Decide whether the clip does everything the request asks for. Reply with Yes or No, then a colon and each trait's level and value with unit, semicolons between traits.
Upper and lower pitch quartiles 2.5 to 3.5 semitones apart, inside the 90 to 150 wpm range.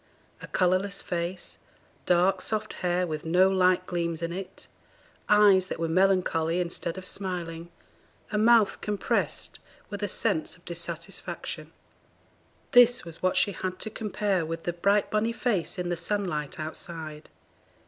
Yes: average, 2.8 semitones; average, 145 wpm